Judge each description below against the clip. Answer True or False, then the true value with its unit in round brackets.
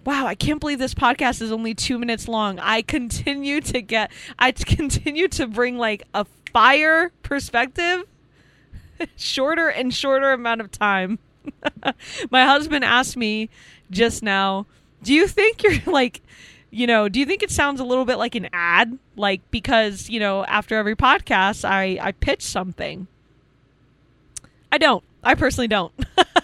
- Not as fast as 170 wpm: True (155 wpm)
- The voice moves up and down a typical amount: False (5.8 semitones)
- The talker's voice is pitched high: True (235 Hz)